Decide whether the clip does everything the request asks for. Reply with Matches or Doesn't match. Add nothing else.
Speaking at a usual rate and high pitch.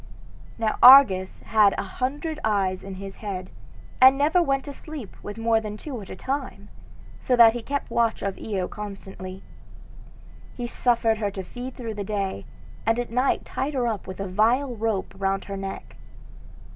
Matches